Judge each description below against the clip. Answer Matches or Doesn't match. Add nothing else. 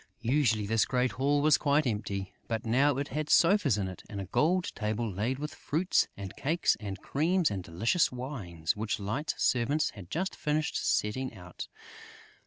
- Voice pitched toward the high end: Doesn't match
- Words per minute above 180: Doesn't match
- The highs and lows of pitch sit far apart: Matches